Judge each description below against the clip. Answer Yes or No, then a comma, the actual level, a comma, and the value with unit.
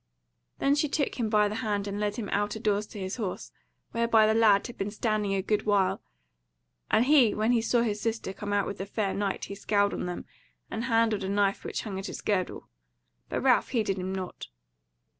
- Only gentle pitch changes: Yes, narrow, 2.1 semitones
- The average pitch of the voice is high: Yes, high, 210 Hz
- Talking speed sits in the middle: No, fast, 220 wpm